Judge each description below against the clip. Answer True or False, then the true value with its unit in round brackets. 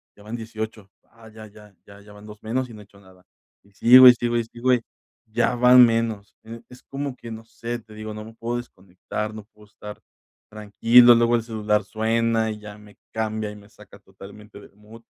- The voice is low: True (110 Hz)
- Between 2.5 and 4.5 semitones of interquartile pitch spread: False (1.9 semitones)